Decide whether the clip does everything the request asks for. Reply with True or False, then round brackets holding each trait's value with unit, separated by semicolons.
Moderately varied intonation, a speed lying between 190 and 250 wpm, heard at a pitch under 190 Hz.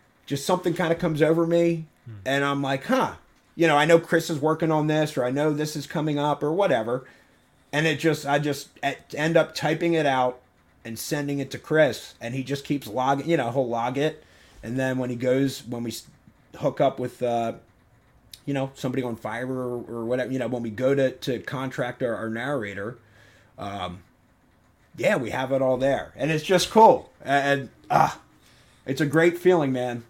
True (4.0 semitones; 205 wpm; 135 Hz)